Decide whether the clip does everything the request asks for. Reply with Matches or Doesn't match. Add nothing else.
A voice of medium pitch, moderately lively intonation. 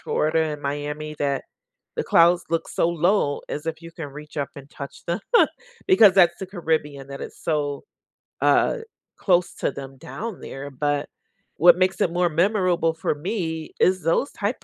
Matches